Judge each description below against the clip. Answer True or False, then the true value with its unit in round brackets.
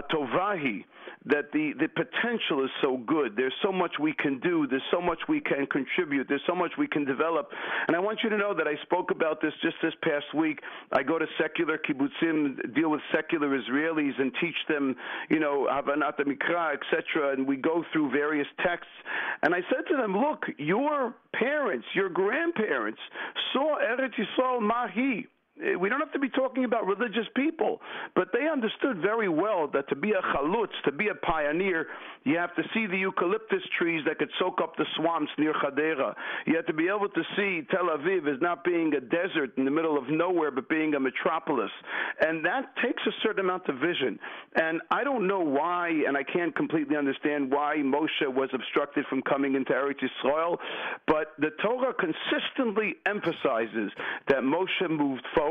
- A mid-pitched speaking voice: True (165 Hz)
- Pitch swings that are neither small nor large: False (7.5 semitones)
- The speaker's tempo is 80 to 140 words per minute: False (190 wpm)